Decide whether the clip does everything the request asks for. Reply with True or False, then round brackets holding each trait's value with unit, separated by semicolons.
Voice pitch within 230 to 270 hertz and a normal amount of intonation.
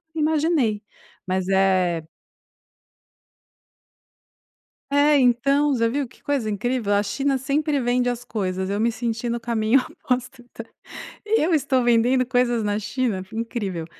True (240 Hz; 4.0 semitones)